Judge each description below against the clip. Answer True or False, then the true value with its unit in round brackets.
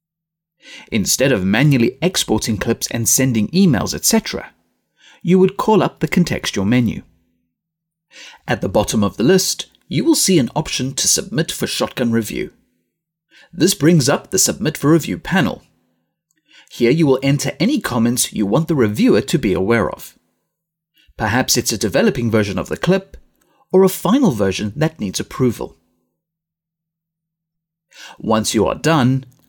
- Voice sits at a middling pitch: True (160 Hz)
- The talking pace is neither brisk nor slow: True (150 wpm)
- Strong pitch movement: True (7.1 semitones)